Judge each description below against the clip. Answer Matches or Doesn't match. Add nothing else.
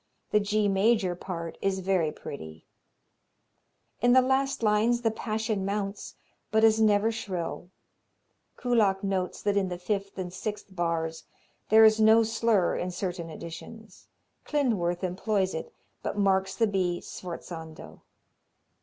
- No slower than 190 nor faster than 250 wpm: Doesn't match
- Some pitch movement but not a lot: Matches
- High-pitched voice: Matches